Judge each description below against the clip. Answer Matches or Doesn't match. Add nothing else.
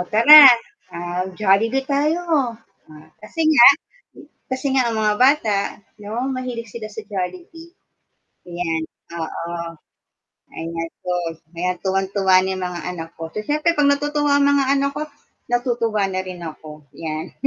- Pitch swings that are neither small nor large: Doesn't match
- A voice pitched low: Doesn't match